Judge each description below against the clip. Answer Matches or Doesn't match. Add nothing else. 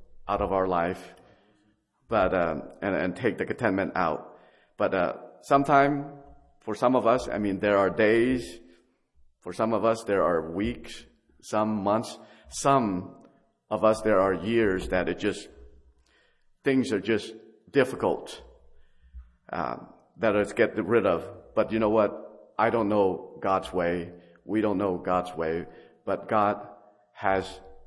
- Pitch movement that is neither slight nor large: Matches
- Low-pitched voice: Matches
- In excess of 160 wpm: Doesn't match